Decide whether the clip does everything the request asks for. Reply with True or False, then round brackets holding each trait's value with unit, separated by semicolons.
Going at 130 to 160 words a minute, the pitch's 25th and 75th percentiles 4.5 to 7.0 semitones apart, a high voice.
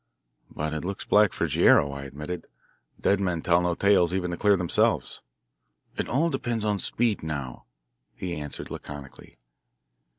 False (155 wpm; 5.0 semitones; 90 Hz)